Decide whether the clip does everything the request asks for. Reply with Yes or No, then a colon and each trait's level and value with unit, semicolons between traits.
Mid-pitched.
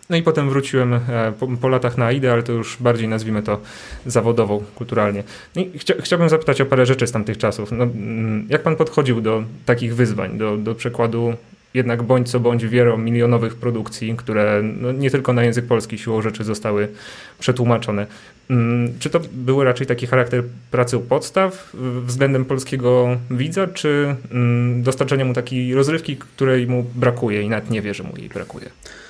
No: low, 120 Hz